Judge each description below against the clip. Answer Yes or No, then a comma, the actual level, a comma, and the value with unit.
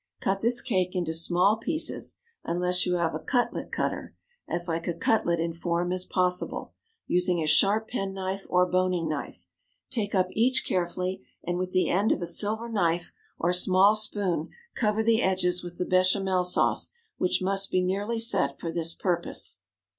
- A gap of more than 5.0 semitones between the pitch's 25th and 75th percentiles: No, narrow, 2.4 semitones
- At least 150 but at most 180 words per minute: Yes, average, 170 wpm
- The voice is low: No, medium, 185 Hz